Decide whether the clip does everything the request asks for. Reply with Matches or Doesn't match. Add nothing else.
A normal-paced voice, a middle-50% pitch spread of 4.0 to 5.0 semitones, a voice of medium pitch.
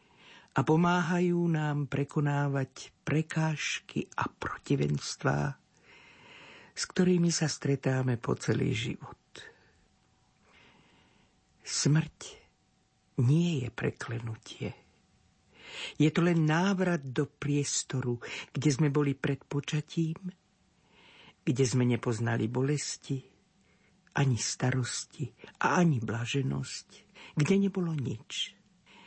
Doesn't match